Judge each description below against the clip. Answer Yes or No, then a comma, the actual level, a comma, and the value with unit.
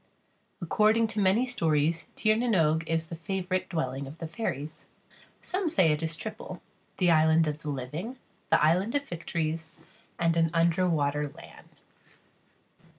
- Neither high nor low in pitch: Yes, medium, 165 Hz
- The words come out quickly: No, average, 150 wpm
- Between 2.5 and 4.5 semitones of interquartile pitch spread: Yes, average, 3.5 semitones